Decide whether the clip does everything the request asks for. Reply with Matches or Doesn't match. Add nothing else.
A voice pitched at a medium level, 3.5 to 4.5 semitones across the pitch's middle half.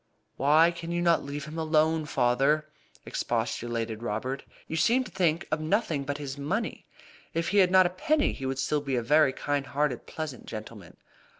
Matches